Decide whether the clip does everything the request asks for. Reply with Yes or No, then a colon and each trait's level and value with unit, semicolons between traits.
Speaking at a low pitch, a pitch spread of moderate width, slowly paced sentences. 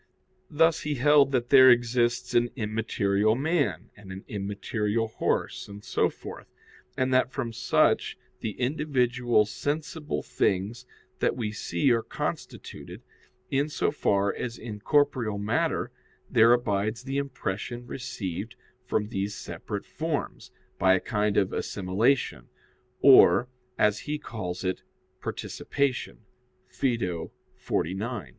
Yes: low, 115 Hz; average, 4.2 semitones; slow, 125 wpm